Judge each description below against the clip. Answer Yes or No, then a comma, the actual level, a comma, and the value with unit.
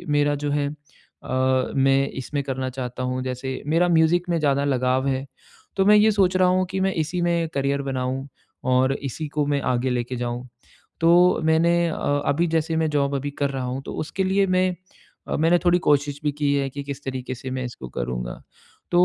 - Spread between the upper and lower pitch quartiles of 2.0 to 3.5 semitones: No, average, 4.0 semitones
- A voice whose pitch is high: No, medium, 140 Hz